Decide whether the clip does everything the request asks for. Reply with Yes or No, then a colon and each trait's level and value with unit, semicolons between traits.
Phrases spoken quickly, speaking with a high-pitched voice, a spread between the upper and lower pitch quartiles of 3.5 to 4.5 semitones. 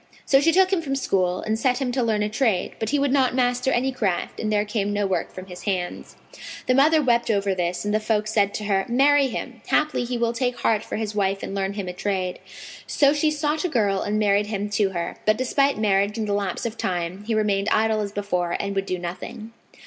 Yes: fast, 250 wpm; high, 215 Hz; average, 4.2 semitones